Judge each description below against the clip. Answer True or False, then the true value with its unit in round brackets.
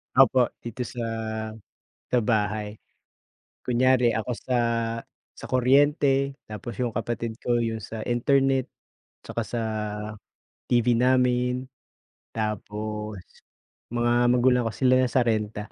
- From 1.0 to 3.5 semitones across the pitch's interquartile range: True (2.5 semitones)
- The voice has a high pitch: False (120 Hz)